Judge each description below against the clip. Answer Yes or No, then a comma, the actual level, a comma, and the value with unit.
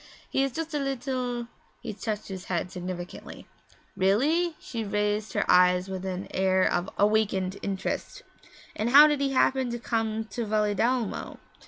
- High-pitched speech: Yes, high, 215 Hz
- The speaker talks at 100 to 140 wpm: No, average, 160 wpm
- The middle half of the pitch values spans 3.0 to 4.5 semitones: No, average, 5.1 semitones